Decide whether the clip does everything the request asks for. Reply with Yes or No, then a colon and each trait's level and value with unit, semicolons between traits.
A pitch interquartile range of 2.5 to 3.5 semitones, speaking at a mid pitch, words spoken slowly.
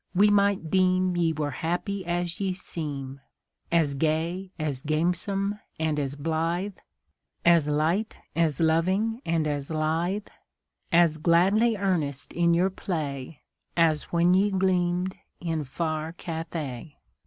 Yes: average, 3.1 semitones; medium, 170 Hz; slow, 125 wpm